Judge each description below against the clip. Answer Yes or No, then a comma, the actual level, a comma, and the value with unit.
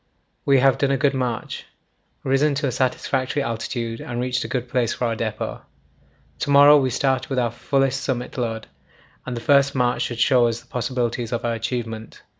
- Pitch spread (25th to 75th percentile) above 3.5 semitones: No, narrow, 2.5 semitones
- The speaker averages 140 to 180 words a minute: No, average, 195 wpm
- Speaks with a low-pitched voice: Yes, low, 125 Hz